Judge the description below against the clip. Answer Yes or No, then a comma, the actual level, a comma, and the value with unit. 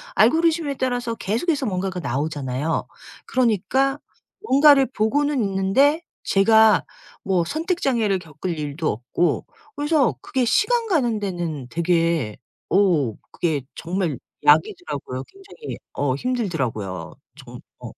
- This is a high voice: Yes, high, 195 Hz